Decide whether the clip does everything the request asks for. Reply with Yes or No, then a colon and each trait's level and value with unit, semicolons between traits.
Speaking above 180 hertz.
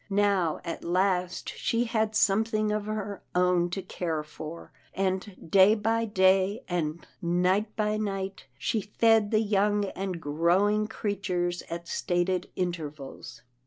Yes: high, 190 Hz